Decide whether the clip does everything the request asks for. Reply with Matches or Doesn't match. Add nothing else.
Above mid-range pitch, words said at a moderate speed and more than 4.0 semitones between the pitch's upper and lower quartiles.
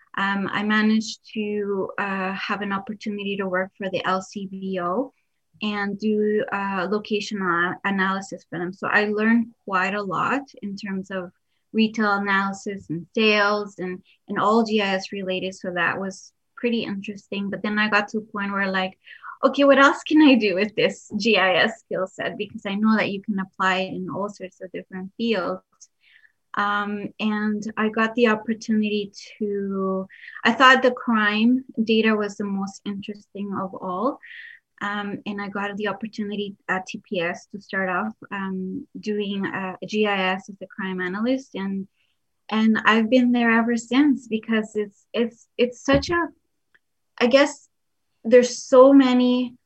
Doesn't match